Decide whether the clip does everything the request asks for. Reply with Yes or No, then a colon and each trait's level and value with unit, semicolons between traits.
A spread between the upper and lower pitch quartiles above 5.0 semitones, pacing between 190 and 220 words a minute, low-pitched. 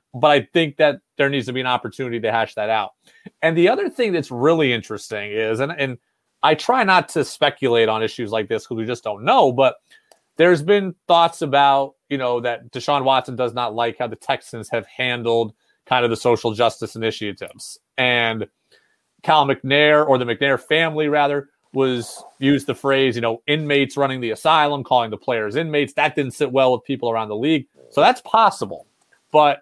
No: average, 3.7 semitones; average, 195 wpm; low, 130 Hz